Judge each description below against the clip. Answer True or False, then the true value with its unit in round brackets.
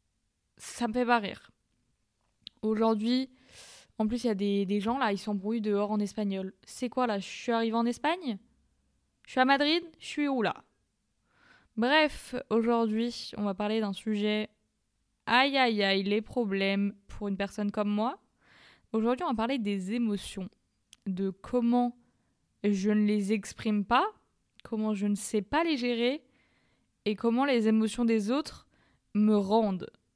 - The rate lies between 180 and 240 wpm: False (160 wpm)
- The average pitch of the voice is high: True (220 Hz)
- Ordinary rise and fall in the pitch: True (3.0 semitones)